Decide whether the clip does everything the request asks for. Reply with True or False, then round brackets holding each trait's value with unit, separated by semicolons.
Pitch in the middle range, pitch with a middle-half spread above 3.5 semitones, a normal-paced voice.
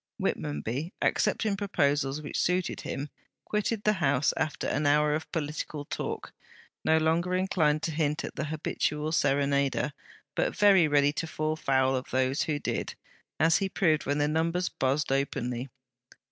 False (150 Hz; 2.7 semitones; 155 wpm)